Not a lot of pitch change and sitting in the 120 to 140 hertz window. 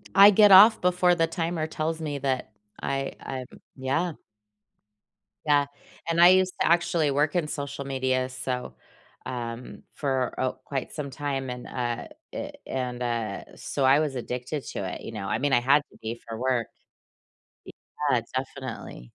No: average, 3.9 semitones; low, 135 Hz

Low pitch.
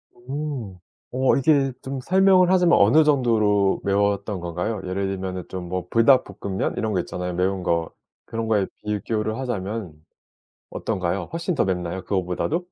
Yes: low, 105 Hz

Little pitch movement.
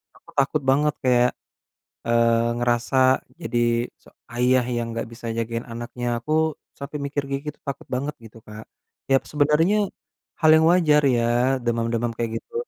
No: average, 4.1 semitones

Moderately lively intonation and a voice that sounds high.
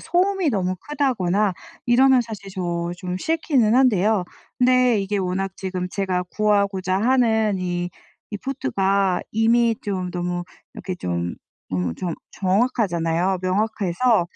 Yes: average, 4.7 semitones; high, 195 Hz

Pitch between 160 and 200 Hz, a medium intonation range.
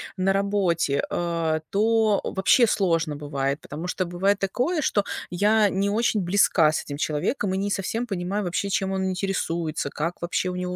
Yes: high, 190 Hz; average, 3.3 semitones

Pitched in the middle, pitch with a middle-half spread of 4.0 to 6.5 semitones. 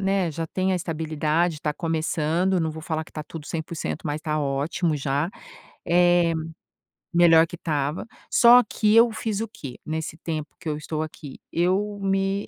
No: medium, 165 Hz; average, 3.3 semitones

